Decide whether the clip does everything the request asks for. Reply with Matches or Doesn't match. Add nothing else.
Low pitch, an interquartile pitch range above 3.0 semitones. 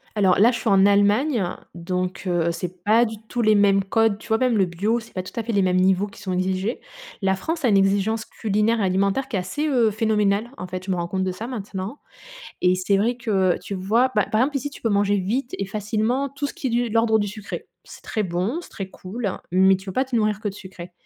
Doesn't match